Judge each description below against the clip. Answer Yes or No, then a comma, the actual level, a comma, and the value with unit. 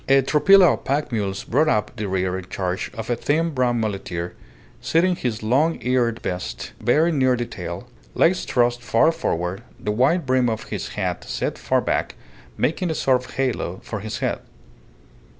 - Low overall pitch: Yes, low, 120 Hz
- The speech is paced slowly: No, average, 180 wpm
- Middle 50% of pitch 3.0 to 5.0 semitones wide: No, wide, 5.5 semitones